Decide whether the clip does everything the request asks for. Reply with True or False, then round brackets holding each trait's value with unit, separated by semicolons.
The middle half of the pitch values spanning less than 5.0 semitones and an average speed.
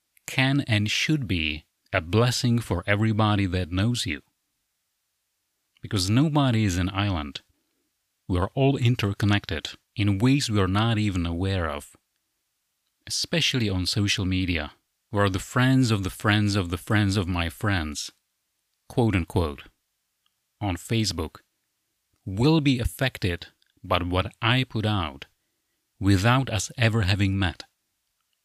False (3.9 semitones; 130 wpm)